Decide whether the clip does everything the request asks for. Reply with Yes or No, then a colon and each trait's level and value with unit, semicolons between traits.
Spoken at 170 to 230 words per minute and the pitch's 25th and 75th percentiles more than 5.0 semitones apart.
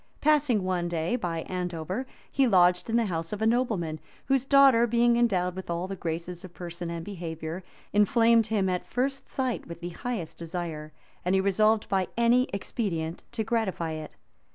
Yes: average, 175 wpm; wide, 5.4 semitones